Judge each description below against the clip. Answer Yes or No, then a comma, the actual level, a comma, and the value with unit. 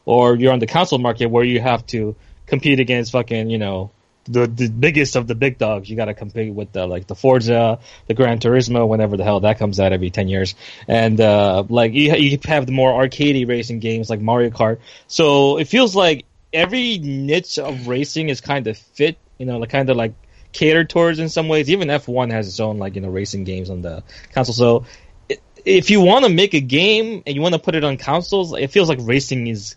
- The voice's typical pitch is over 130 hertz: No, low, 125 Hz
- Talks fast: Yes, fast, 230 wpm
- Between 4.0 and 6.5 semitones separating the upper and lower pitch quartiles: Yes, average, 4.9 semitones